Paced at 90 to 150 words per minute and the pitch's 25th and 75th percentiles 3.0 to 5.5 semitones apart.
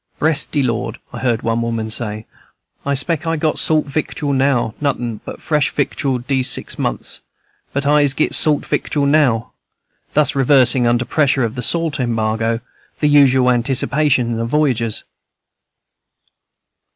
Yes: average, 145 wpm; average, 3.8 semitones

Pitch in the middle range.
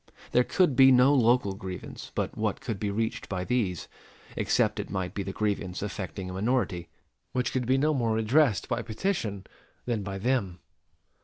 No: low, 110 Hz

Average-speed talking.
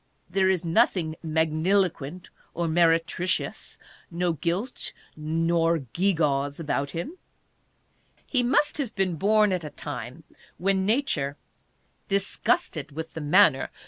No: slow, 125 wpm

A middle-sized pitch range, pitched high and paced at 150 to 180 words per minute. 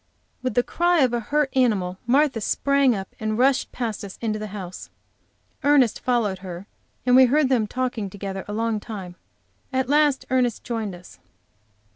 Yes: average, 4.2 semitones; high, 235 Hz; average, 170 wpm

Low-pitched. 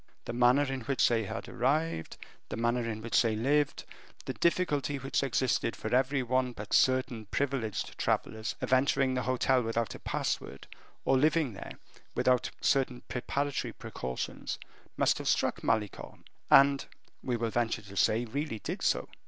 Yes: low, 125 Hz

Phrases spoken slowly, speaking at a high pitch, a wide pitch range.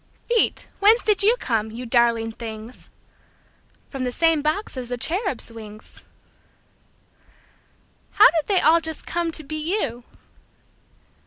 Yes: slow, 120 wpm; very high, 290 Hz; wide, 6.8 semitones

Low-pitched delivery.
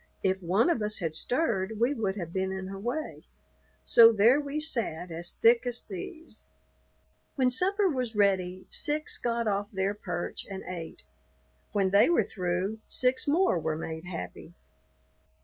No: high, 205 Hz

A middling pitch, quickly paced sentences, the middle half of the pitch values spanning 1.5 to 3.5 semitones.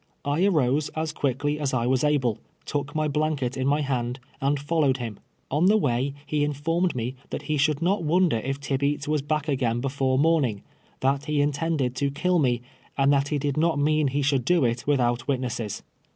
Yes: medium, 145 Hz; fast, 210 wpm; narrow, 2.6 semitones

